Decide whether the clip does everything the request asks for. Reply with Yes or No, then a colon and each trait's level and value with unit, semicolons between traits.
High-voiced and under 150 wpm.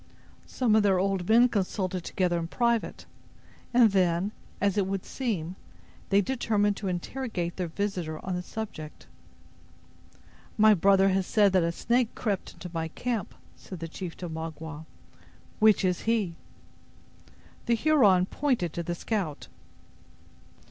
Yes: high, 195 Hz; average, 140 wpm